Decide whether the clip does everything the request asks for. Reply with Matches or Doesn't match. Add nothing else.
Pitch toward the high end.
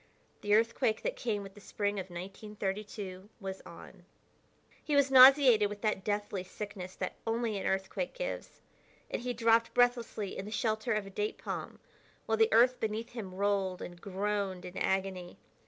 Matches